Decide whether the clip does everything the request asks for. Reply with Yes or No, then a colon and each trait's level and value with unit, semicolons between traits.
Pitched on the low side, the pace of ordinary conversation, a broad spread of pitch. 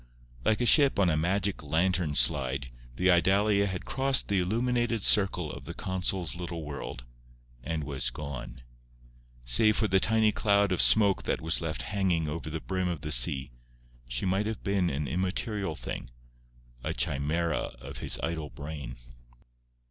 No: very low, 90 Hz; average, 160 wpm; average, 5.0 semitones